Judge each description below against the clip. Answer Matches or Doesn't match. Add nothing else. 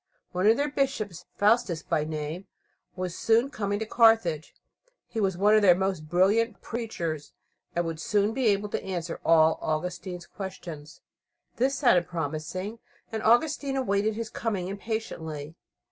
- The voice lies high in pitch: Matches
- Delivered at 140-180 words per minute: Matches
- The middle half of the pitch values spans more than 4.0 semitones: Matches